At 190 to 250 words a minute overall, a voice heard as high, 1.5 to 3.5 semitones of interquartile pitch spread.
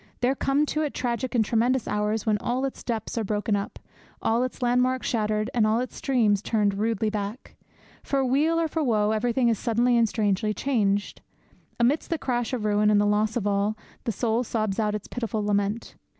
Yes: average, 200 wpm; high, 225 Hz; average, 2.9 semitones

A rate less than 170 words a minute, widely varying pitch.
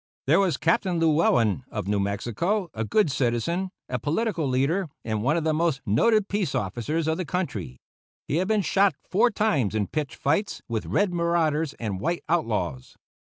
No: average, 175 wpm; wide, 7.8 semitones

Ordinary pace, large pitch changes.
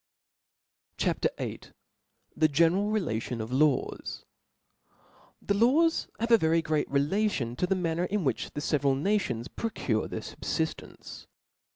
Yes: average, 145 wpm; wide, 6.6 semitones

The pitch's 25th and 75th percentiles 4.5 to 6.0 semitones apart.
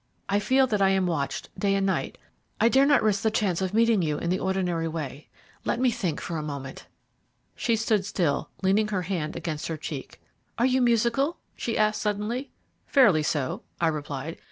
Yes: wide, 5.5 semitones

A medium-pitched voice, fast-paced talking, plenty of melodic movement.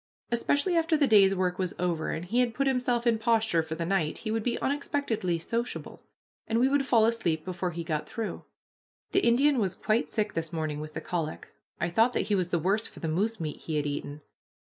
No: high, 205 Hz; fast, 225 wpm; wide, 6.1 semitones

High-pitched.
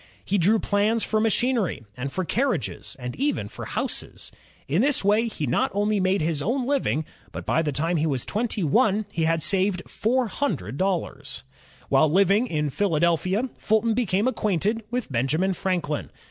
Yes: high, 195 Hz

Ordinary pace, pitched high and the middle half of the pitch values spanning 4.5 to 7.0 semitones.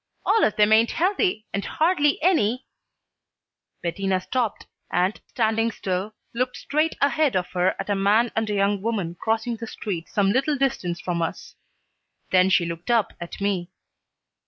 Yes: average, 165 wpm; high, 215 Hz; average, 4.9 semitones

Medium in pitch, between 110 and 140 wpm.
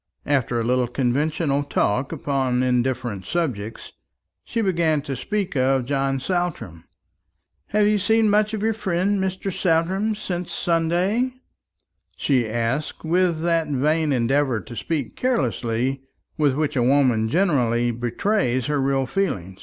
Yes: medium, 145 Hz; slow, 135 wpm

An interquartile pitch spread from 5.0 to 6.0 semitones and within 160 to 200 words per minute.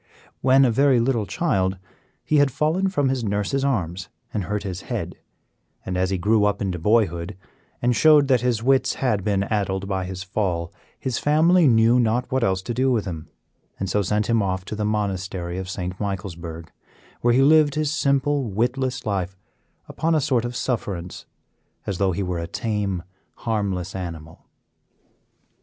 Yes: wide, 5.6 semitones; average, 175 wpm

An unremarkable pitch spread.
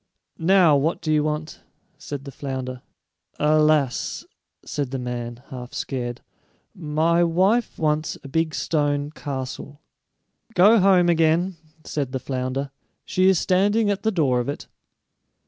Yes: average, 4.4 semitones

